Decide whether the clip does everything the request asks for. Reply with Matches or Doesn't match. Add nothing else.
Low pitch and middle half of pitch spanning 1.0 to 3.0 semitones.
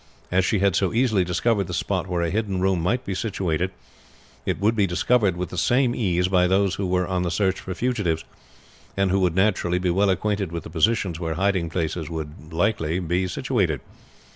Matches